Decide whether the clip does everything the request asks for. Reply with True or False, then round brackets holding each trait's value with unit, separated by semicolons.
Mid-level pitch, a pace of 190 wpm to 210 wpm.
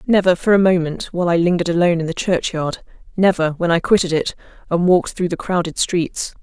True (175 Hz; 205 wpm)